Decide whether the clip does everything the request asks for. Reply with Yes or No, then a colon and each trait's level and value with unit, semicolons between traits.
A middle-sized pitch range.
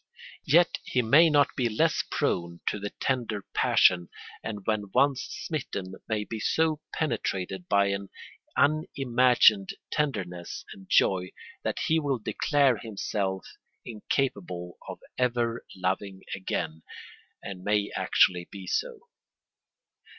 No: wide, 5.9 semitones